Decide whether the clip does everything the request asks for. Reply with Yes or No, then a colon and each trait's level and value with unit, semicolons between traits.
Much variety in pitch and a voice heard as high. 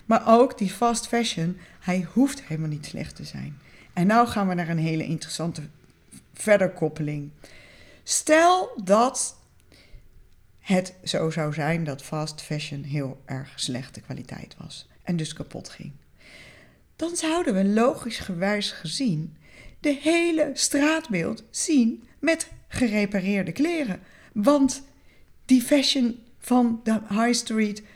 Yes: wide, 7.8 semitones; high, 200 Hz